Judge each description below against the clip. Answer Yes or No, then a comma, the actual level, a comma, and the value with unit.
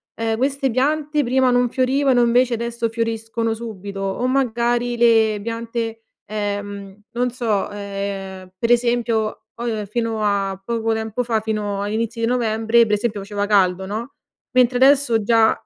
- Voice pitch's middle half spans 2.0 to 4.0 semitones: Yes, narrow, 2.6 semitones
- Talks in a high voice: Yes, high, 230 Hz